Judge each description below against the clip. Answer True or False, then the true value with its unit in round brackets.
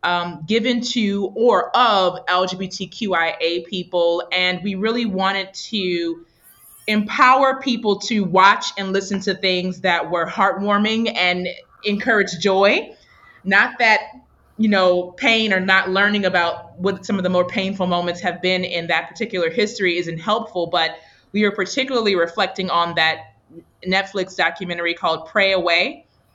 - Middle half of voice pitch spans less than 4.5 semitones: True (2.8 semitones)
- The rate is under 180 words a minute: True (140 wpm)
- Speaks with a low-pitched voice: False (190 Hz)